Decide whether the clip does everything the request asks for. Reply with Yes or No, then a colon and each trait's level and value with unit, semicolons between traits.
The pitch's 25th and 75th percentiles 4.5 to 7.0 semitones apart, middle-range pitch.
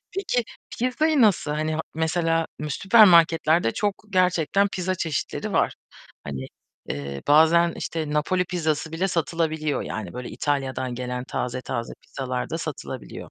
Yes: average, 5.2 semitones; medium, 160 Hz